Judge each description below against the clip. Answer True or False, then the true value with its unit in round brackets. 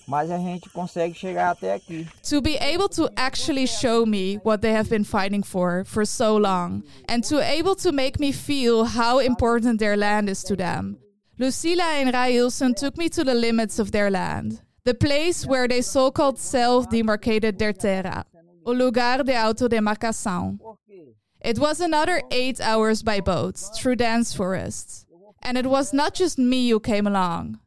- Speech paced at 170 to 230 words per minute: False (155 wpm)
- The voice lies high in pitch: True (225 Hz)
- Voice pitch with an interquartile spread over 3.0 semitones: True (5.0 semitones)